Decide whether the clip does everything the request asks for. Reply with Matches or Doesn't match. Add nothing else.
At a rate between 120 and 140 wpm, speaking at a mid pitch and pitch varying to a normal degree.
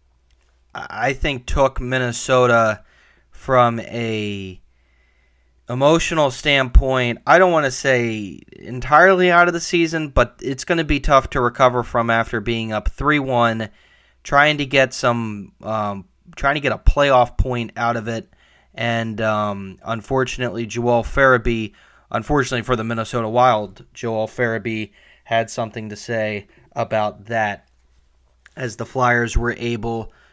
Doesn't match